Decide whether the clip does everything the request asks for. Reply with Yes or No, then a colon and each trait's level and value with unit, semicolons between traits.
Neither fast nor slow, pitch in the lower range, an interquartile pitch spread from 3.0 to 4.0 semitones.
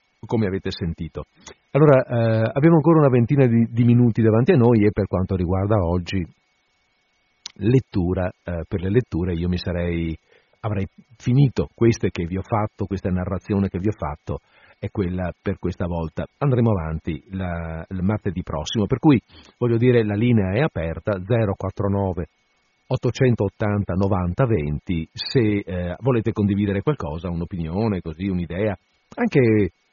No: average, 145 wpm; low, 100 Hz; average, 4.4 semitones